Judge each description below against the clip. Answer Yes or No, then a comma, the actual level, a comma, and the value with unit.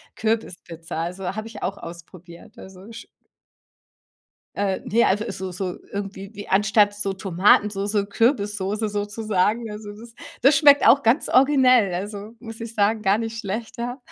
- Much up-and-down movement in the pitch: No, average, 2.8 semitones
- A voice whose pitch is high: Yes, high, 205 Hz